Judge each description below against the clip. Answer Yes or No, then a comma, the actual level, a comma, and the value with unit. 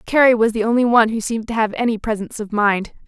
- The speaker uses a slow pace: No, fast, 255 wpm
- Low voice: No, high, 225 Hz